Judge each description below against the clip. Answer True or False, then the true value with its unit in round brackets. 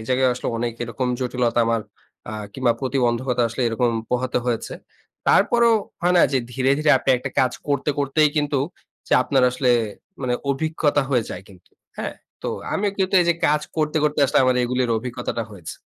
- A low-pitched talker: True (130 Hz)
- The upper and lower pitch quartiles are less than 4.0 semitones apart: True (3.3 semitones)